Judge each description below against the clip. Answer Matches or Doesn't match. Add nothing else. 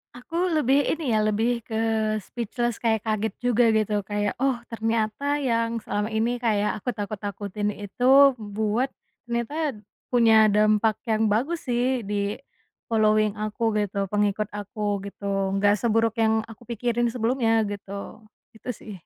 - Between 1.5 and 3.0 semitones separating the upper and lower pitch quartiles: Matches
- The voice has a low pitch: Doesn't match